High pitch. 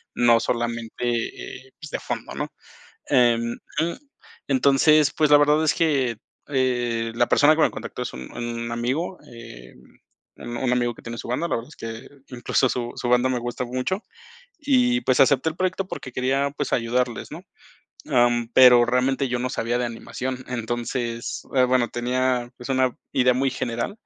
No: low, 125 Hz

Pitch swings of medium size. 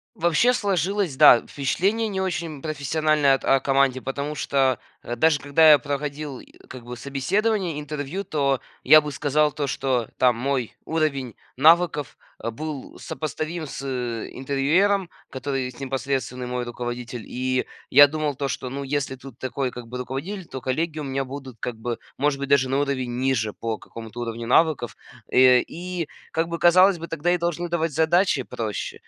Yes: average, 3.7 semitones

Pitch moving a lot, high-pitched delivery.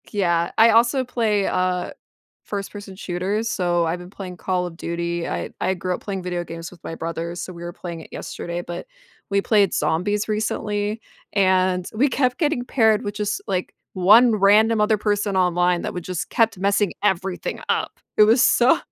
No: average, 3.2 semitones; high, 195 Hz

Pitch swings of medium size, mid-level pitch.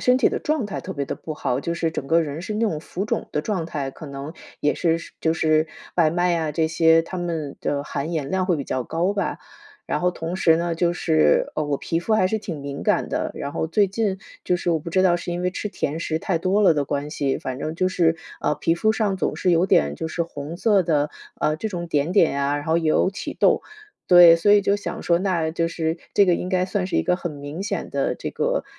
Yes: average, 3.1 semitones; medium, 165 Hz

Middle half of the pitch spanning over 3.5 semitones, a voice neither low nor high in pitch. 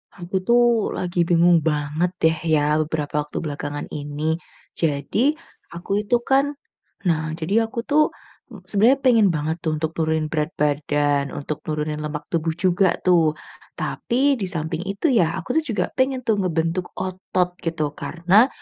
Yes: average, 4.5 semitones; medium, 165 Hz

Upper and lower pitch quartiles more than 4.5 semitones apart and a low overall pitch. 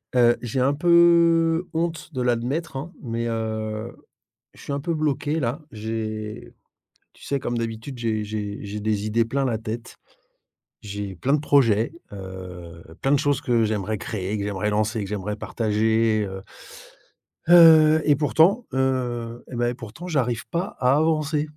Yes: average, 5.3 semitones; low, 120 Hz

